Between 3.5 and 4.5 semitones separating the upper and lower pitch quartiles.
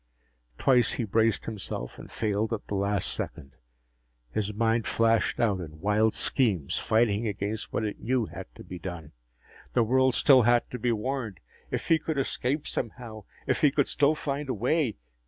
Yes: average, 3.8 semitones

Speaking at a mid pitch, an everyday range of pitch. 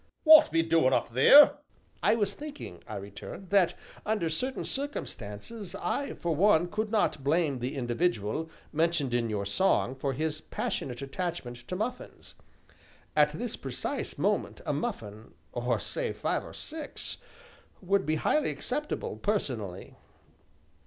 No: medium, 160 Hz; wide, 8.8 semitones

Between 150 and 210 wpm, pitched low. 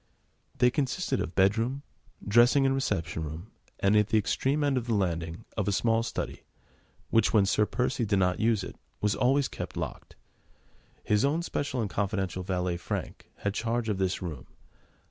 Yes: average, 175 wpm; low, 105 Hz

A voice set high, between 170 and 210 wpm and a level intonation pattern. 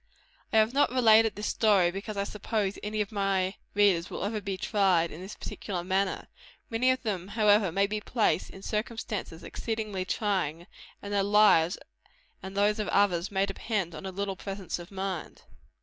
Yes: high, 200 Hz; average, 180 wpm; narrow, 2.1 semitones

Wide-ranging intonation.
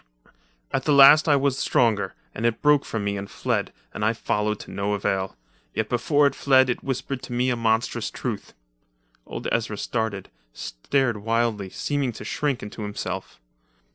No: average, 4.4 semitones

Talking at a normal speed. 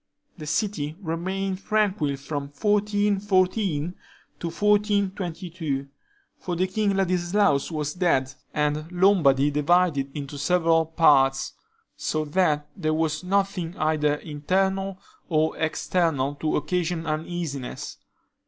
No: slow, 100 wpm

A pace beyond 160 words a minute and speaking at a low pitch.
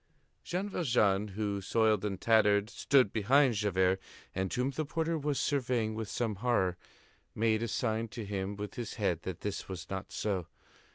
Yes: average, 170 wpm; low, 110 Hz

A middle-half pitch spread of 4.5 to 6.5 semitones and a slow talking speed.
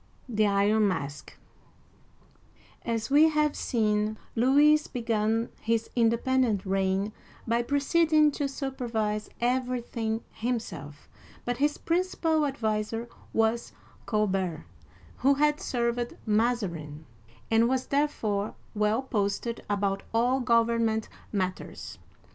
No: average, 3.7 semitones; slow, 100 wpm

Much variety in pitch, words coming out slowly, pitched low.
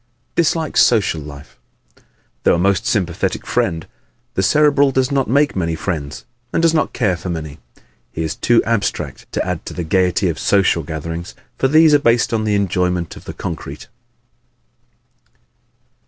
No: wide, 7.8 semitones; average, 165 wpm; very low, 95 Hz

